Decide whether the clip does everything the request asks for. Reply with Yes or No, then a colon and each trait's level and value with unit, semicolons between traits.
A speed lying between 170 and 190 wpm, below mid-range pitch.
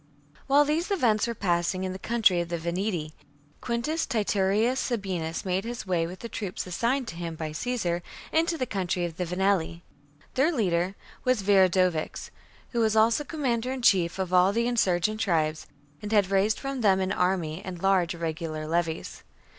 No: average, 175 wpm; high, 190 Hz